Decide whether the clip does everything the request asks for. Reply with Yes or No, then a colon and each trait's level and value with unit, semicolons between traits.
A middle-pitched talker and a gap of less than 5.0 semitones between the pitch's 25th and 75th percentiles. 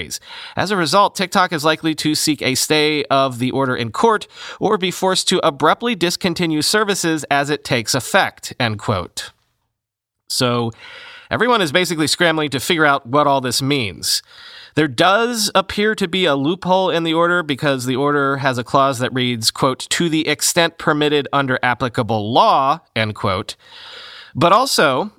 No: medium, 150 Hz; wide, 5.6 semitones